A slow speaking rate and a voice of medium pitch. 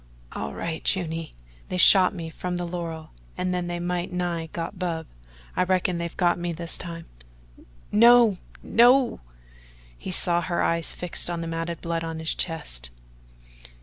No: average, 155 wpm; medium, 175 Hz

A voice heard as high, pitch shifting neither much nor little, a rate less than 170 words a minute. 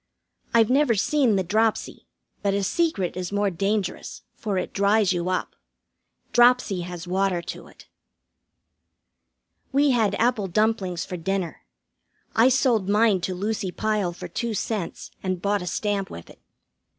Yes: high, 200 Hz; average, 3.3 semitones; average, 150 wpm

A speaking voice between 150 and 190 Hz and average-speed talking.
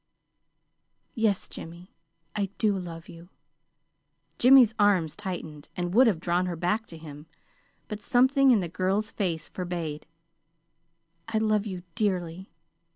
No: medium, 185 Hz; slow, 130 wpm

